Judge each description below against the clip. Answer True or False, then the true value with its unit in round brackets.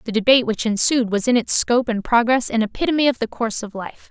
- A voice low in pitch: False (230 Hz)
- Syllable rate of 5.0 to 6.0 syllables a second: False (6.6 syllables/s)